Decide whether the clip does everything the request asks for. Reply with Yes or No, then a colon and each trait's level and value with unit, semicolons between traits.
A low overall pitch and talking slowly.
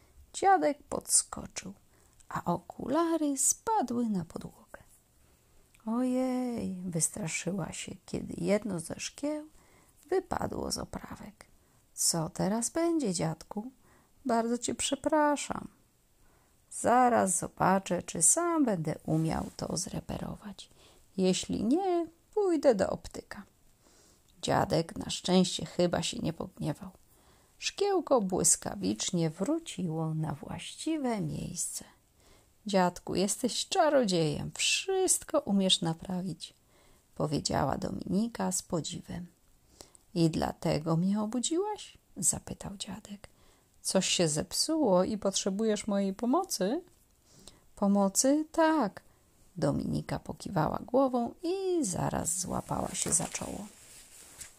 No: high, 215 Hz; slow, 90 wpm